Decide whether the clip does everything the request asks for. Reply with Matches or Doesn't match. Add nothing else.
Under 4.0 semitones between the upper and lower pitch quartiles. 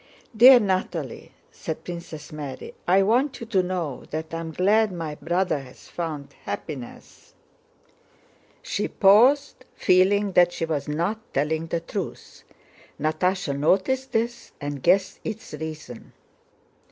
Doesn't match